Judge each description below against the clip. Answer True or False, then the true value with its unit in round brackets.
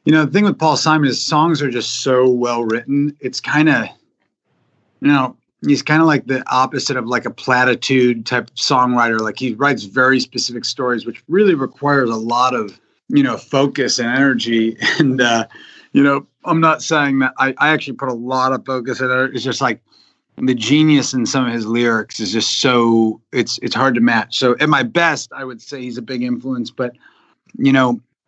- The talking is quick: True (210 wpm)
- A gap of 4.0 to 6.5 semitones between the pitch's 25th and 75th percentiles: False (2.7 semitones)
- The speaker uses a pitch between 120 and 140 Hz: True (130 Hz)